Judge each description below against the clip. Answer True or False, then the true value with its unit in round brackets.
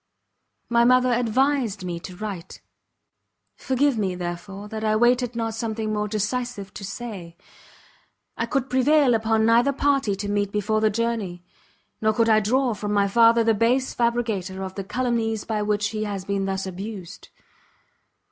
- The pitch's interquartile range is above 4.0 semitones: False (3.1 semitones)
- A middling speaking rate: True (160 wpm)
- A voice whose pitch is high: True (220 Hz)